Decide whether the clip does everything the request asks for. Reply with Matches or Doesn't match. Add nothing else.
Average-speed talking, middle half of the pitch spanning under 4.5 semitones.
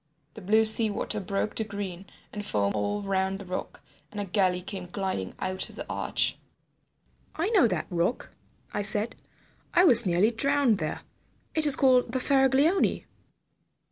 Doesn't match